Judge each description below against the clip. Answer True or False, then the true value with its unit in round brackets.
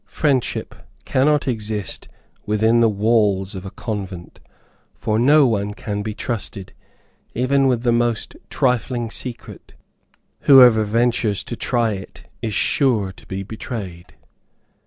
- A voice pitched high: False (110 Hz)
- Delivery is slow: True (125 wpm)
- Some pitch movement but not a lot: True (3.1 semitones)